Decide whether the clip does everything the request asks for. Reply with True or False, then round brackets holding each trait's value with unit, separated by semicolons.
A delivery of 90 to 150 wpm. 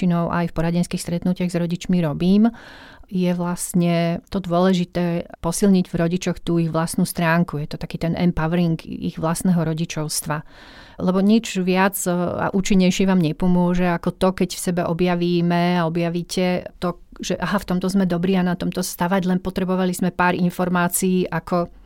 False (160 wpm)